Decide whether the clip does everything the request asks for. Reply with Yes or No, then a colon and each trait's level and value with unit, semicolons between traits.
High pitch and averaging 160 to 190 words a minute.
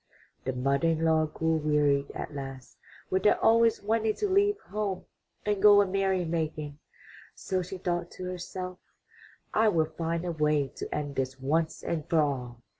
No: medium, 165 Hz; average, 180 wpm